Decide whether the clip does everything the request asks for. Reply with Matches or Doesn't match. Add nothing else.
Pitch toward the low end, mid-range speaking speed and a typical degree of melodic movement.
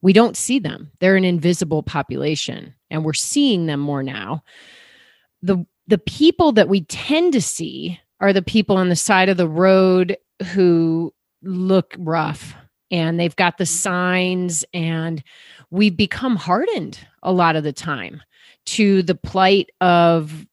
Doesn't match